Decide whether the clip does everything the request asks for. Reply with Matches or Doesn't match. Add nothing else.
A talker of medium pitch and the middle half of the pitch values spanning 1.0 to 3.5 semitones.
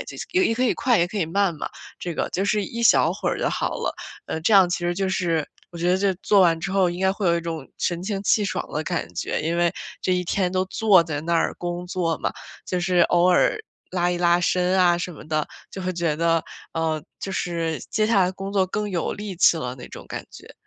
Matches